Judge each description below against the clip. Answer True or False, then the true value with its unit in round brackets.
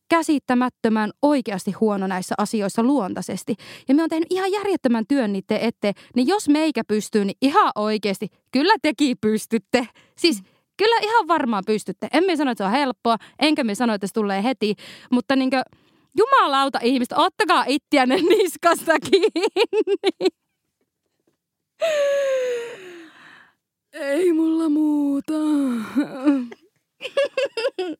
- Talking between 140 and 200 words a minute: False (120 wpm)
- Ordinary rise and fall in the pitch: False (6.9 semitones)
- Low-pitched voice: False (280 Hz)